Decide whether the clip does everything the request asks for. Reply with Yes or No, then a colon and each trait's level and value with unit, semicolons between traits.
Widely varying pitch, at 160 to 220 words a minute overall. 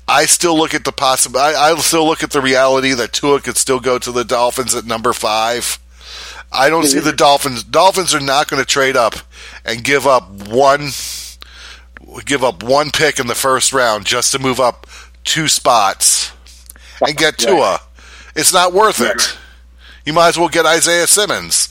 Yes: wide, 6.5 semitones; average, 185 wpm